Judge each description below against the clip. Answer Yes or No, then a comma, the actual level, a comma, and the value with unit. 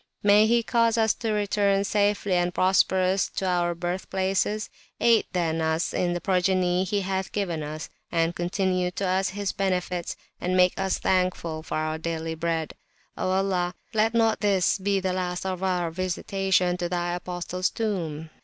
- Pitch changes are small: Yes, narrow, 2.0 semitones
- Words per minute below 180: Yes, average, 170 wpm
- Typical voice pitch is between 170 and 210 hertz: Yes, medium, 185 Hz